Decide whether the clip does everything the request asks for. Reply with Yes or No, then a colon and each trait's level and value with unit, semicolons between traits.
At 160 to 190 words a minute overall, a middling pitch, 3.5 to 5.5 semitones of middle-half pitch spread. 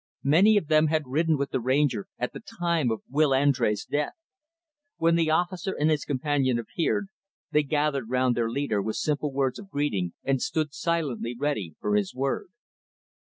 Yes: average, 175 wpm; medium, 145 Hz; average, 3.8 semitones